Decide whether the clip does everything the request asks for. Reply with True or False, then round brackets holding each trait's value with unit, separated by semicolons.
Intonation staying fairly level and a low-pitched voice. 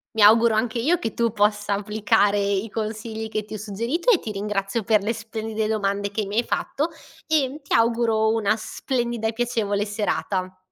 False (2.1 semitones; 220 Hz)